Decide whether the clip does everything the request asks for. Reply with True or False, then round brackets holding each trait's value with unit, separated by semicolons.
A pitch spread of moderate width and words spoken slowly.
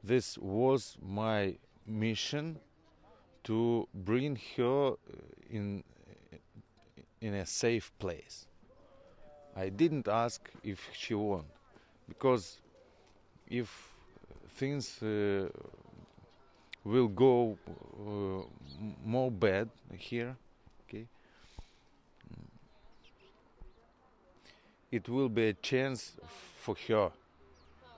True (4.2 semitones; 75 wpm)